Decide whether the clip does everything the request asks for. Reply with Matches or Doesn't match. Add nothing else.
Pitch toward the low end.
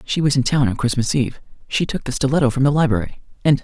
Matches